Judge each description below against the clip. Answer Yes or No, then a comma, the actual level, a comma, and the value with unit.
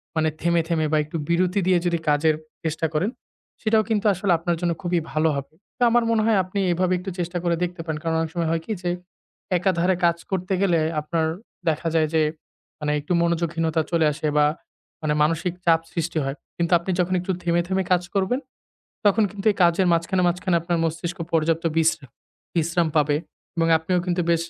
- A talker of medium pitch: Yes, medium, 170 Hz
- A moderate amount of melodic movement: No, narrow, 2.0 semitones